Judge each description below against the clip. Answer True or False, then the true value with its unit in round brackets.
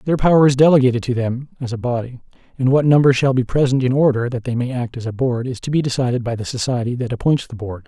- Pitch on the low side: True (125 Hz)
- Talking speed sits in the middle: False (265 wpm)